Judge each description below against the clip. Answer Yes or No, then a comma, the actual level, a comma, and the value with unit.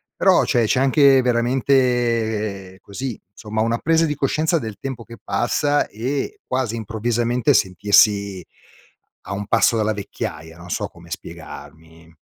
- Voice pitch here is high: No, low, 115 Hz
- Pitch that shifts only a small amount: No, average, 4.3 semitones